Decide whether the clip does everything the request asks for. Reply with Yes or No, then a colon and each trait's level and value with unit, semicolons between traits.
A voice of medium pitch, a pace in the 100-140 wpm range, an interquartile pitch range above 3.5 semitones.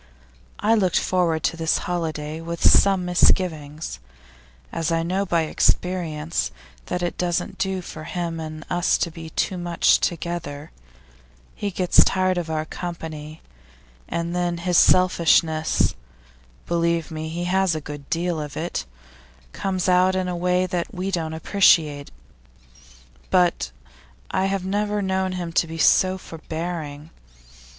No: medium, 170 Hz; slow, 135 wpm; narrow, 2.4 semitones